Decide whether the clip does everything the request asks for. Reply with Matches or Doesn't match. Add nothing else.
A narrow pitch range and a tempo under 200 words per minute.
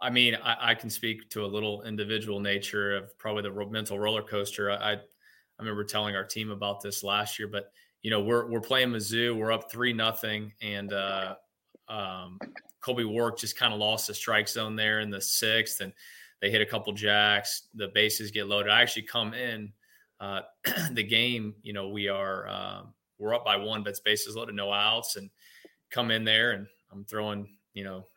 Doesn't match